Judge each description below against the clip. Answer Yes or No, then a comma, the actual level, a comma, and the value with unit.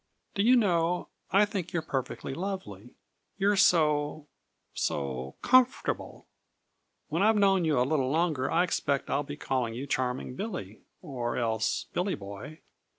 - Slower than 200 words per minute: Yes, average, 145 wpm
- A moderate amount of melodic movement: No, wide, 6.9 semitones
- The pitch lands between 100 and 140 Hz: No, medium, 150 Hz